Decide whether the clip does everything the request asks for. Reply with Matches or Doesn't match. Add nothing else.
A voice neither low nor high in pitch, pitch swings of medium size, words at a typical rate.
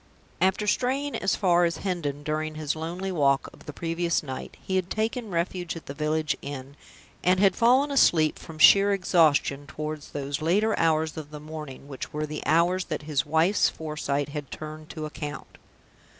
Matches